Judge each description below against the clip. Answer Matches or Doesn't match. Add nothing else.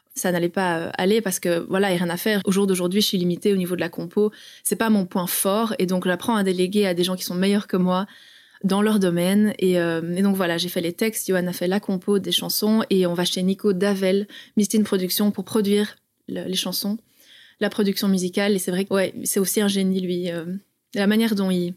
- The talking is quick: Matches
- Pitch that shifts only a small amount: Matches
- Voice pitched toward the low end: Doesn't match